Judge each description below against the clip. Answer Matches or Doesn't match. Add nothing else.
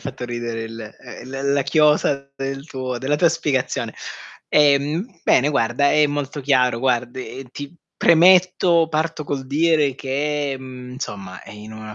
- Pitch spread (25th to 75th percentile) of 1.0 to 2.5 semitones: Doesn't match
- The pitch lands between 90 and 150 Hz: Matches